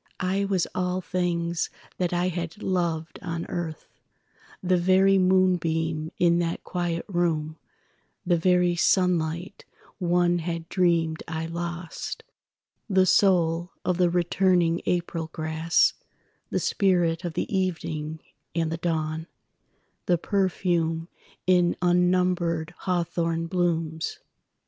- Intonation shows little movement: Yes, narrow, 1.6 semitones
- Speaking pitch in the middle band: Yes, medium, 175 Hz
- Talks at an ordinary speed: No, slow, 100 wpm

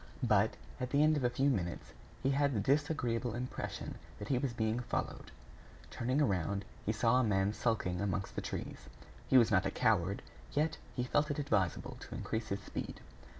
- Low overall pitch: Yes, low, 120 Hz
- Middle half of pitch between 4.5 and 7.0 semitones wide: Yes, average, 5.2 semitones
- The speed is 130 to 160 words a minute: No, average, 190 wpm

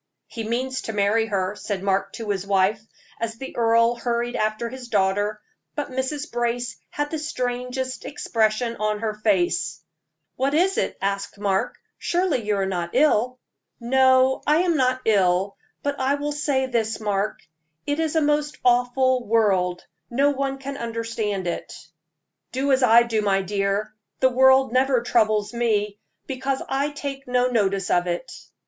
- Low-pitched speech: No, high, 235 Hz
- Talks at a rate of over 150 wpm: Yes, average, 160 wpm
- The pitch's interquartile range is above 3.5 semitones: Yes, average, 4.0 semitones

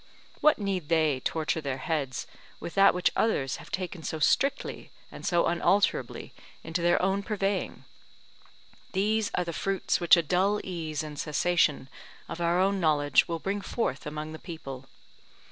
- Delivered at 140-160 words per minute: Yes, average, 155 wpm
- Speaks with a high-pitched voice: No, medium, 170 Hz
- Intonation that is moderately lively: Yes, average, 4.1 semitones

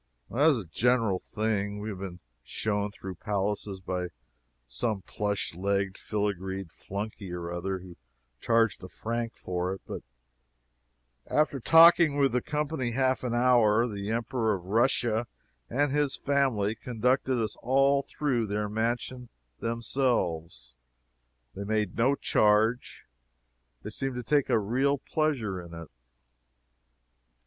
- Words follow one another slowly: Yes, slow, 130 wpm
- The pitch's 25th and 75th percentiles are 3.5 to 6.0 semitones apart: Yes, average, 4.4 semitones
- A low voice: Yes, low, 110 Hz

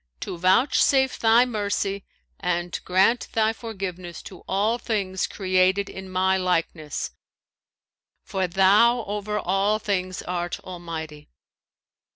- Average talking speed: No, slow, 110 wpm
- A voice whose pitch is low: No, high, 190 Hz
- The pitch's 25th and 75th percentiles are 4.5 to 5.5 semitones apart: No, average, 2.7 semitones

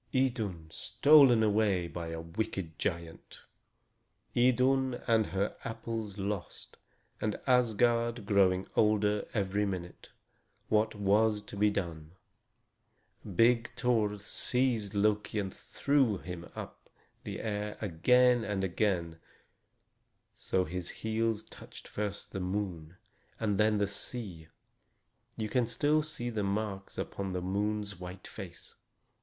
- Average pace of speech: No, slow, 125 wpm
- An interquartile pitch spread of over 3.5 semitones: No, average, 3.2 semitones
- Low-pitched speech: Yes, low, 105 Hz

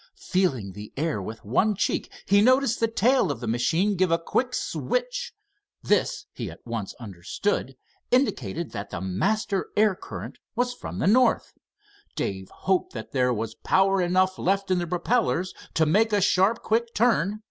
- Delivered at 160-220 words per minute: Yes, average, 165 wpm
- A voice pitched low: No, medium, 185 Hz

